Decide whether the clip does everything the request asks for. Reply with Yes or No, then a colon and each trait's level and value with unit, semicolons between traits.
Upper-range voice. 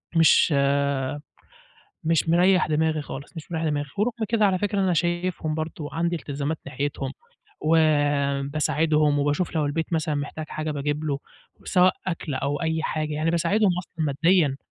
No: medium, 155 Hz